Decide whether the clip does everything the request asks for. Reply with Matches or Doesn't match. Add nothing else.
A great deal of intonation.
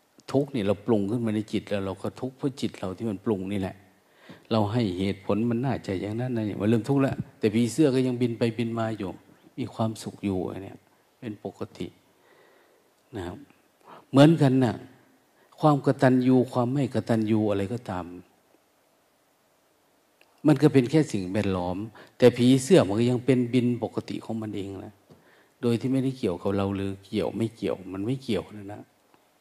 Doesn't match